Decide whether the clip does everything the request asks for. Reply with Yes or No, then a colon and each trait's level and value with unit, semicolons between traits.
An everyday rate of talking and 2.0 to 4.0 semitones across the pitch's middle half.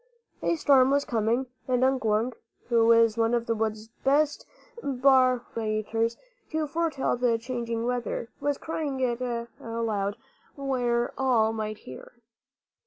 No: slow, 130 wpm; average, 2.8 semitones